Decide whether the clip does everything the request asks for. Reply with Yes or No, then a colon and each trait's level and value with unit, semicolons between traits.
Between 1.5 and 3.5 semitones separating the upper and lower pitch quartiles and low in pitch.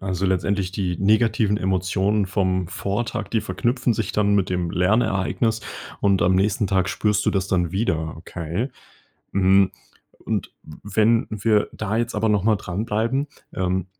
Yes: average, 2.8 semitones; low, 100 Hz